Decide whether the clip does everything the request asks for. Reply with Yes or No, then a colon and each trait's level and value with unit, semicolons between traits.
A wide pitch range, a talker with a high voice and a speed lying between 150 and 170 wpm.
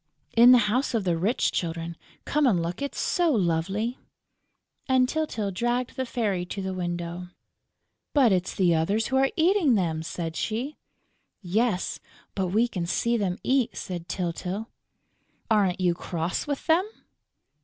Yes: wide, 6.0 semitones; high, 205 Hz; average, 155 wpm